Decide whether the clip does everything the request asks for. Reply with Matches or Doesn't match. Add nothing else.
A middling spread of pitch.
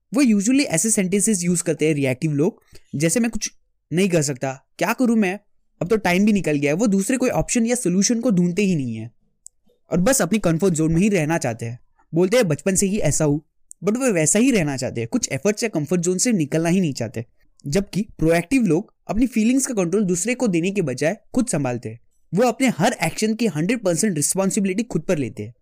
Doesn't match